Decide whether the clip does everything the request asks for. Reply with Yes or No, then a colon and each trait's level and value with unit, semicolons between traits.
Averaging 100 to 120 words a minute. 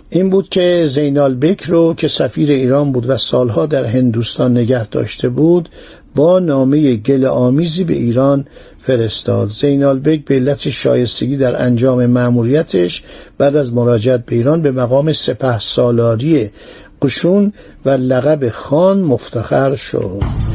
No: average, 135 wpm